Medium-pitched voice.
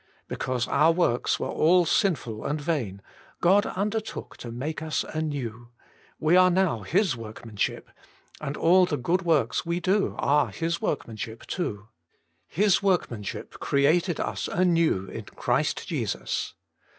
Yes: medium, 155 Hz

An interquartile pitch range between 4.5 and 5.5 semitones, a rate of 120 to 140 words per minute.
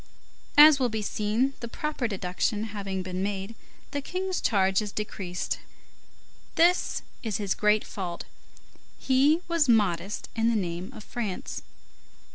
Yes: average, 5.2 semitones; slow, 135 wpm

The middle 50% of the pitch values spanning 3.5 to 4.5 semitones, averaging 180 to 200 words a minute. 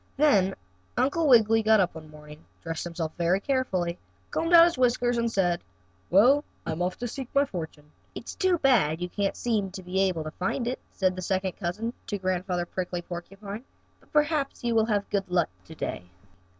No: wide, 5.6 semitones; average, 190 wpm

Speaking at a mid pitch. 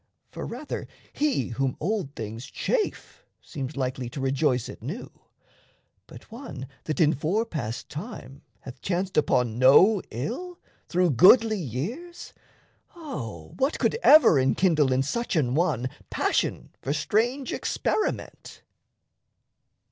Yes: medium, 150 Hz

